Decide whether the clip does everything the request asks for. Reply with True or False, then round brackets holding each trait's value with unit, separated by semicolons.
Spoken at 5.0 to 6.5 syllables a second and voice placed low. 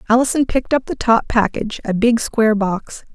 False (5.7 syllables/s; 225 Hz)